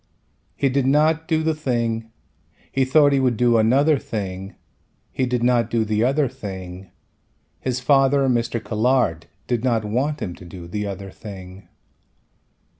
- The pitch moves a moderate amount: Yes, average, 4.5 semitones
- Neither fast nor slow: Yes, average, 155 wpm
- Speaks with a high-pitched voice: No, low, 120 Hz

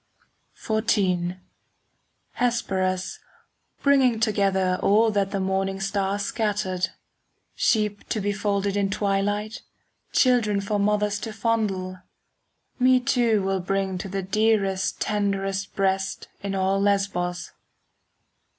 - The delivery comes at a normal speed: No, slow, 110 wpm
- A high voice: Yes, high, 200 Hz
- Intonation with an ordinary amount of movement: No, narrow, 1.8 semitones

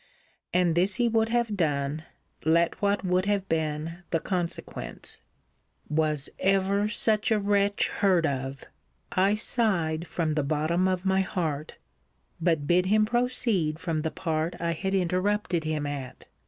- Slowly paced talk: No, average, 145 wpm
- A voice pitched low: No, medium, 180 Hz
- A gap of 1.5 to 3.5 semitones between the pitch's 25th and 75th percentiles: No, average, 4.3 semitones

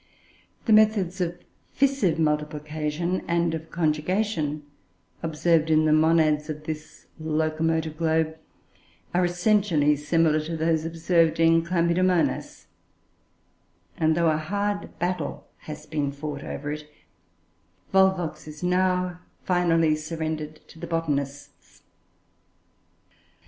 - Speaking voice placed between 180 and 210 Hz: No, medium, 160 Hz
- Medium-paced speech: No, slow, 105 wpm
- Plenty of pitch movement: No, narrow, 2.4 semitones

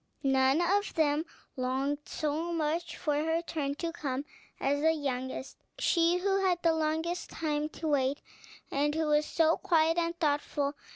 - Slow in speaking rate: No, average, 160 wpm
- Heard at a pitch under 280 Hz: No, very high, 310 Hz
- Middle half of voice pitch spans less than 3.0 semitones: Yes, narrow, 2.6 semitones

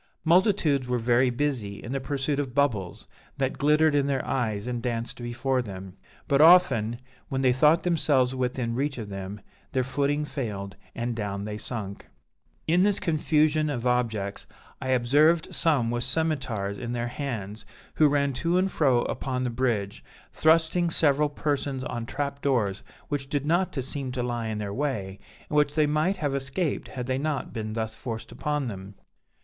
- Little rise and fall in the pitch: No, average, 4.2 semitones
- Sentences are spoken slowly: No, average, 175 wpm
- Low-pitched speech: Yes, low, 130 Hz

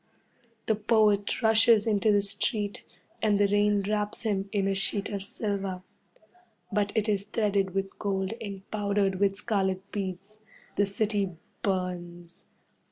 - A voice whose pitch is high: Yes, high, 200 Hz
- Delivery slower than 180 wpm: Yes, average, 140 wpm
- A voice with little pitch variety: Yes, narrow, 1.4 semitones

